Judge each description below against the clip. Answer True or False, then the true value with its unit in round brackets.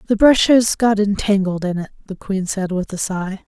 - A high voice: True (200 Hz)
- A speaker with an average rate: False (220 wpm)